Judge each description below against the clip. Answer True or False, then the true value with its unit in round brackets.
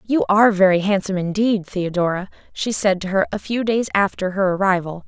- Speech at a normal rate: True (190 wpm)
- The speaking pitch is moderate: False (195 Hz)